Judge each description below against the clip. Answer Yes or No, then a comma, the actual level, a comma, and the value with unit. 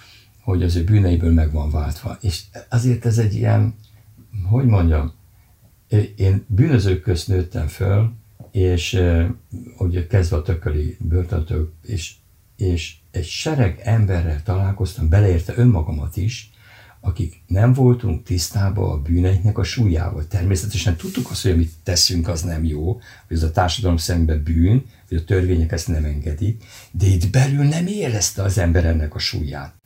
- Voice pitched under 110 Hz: Yes, very low, 95 Hz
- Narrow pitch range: No, average, 4.0 semitones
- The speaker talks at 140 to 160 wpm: Yes, average, 150 wpm